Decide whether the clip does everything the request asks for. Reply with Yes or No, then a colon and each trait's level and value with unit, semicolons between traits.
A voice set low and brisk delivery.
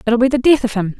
No: high, 240 Hz; fast, 360 wpm